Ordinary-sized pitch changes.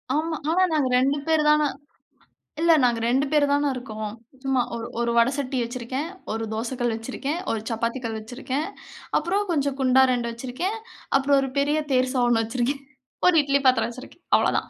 Yes: average, 3.4 semitones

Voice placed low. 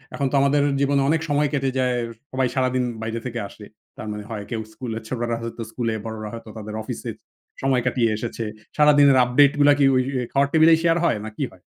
Yes: low, 130 Hz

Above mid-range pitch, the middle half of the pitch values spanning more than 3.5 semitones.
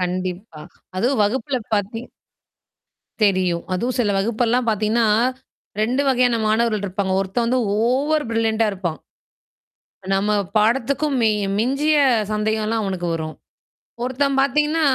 Yes: high, 225 Hz; average, 4.2 semitones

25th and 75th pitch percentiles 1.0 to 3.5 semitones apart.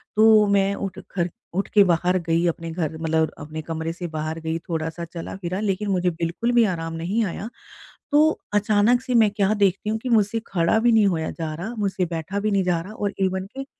No: average, 4.0 semitones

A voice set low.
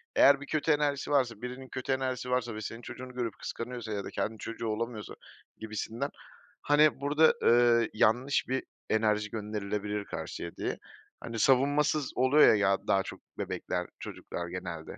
Yes: low, 120 Hz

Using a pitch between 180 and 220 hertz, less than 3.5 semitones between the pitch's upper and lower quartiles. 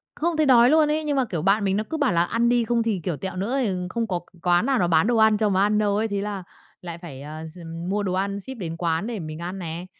No: high, 200 Hz; average, 4.9 semitones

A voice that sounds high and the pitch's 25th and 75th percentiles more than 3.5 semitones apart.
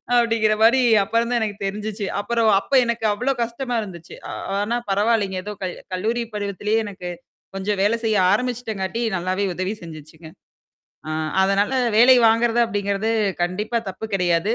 No: high, 210 Hz; average, 3.2 semitones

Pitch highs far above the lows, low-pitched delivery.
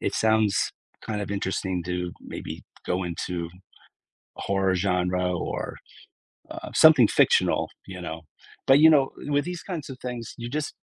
Yes: wide, 6.7 semitones; low, 100 Hz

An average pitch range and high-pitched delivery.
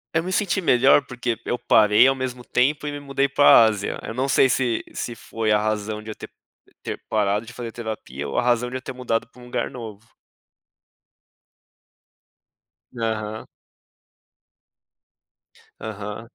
No: average, 3.1 semitones; low, 115 Hz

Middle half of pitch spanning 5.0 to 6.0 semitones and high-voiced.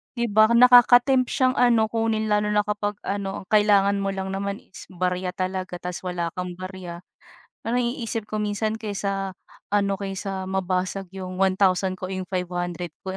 No: narrow, 2.6 semitones; high, 195 Hz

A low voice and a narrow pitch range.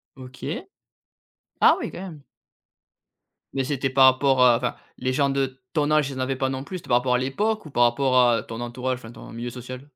Yes: low, 130 Hz; narrow, 1.7 semitones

